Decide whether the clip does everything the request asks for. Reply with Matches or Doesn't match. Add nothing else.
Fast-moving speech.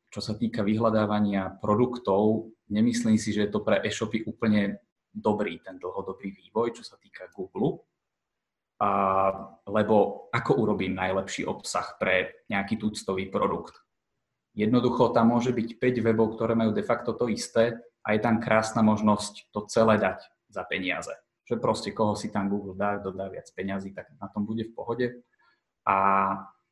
Doesn't match